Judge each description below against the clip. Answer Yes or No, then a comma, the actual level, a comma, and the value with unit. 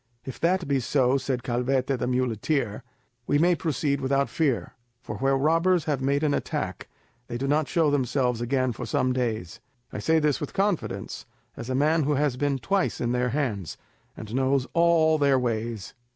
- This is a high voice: No, low, 135 Hz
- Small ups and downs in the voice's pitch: No, average, 3.4 semitones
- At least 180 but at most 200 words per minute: Yes, average, 185 wpm